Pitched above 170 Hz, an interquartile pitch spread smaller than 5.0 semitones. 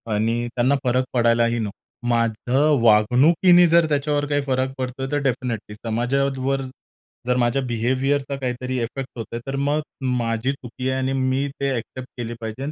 No: low, 130 Hz; narrow, 2.6 semitones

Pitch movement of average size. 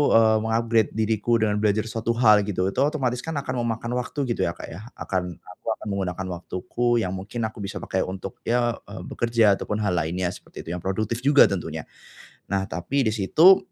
Yes: average, 3.8 semitones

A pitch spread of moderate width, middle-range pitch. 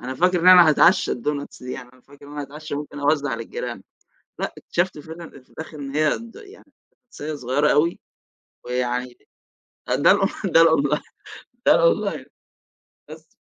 Yes: average, 3.6 semitones; medium, 150 Hz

